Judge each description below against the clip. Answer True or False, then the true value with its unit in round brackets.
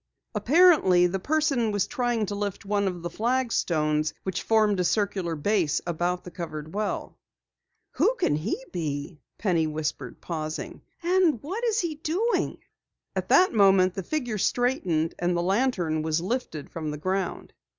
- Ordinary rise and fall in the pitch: False (6.6 semitones)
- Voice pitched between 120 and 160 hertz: False (190 Hz)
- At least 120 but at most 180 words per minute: True (155 wpm)